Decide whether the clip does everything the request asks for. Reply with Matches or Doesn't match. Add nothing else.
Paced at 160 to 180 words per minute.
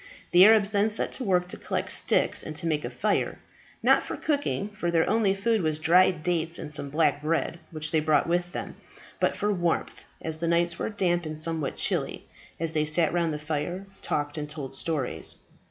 Doesn't match